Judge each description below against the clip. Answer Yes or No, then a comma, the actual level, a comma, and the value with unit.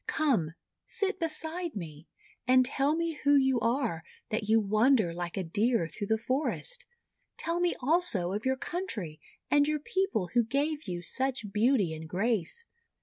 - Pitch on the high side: Yes, very high, 250 Hz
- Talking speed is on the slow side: No, average, 160 wpm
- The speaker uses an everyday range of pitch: No, wide, 7.5 semitones